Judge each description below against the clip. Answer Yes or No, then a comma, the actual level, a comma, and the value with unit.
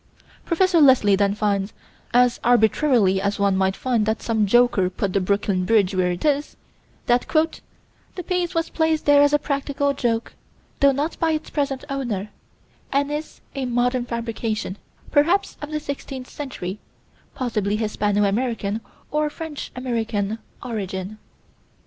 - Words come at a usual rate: Yes, average, 145 wpm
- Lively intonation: Yes, wide, 5.8 semitones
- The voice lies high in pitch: Yes, high, 240 Hz